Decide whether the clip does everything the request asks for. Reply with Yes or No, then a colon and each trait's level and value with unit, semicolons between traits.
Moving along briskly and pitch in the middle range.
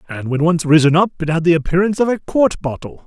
Yes: fast, 255 wpm; medium, 170 Hz